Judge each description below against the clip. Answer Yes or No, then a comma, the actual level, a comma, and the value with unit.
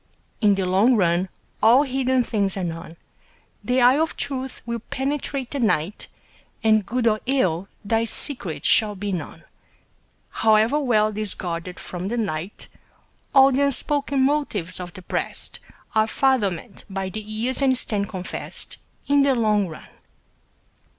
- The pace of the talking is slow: No, average, 150 wpm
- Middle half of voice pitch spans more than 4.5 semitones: Yes, average, 5.3 semitones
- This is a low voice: No, high, 220 Hz